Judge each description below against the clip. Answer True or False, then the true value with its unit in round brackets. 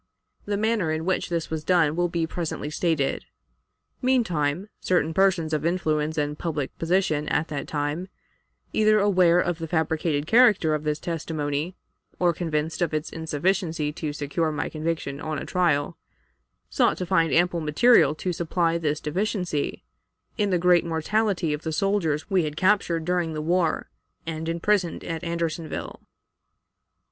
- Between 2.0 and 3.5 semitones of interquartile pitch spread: True (2.7 semitones)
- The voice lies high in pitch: False (165 Hz)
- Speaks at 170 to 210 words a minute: False (155 wpm)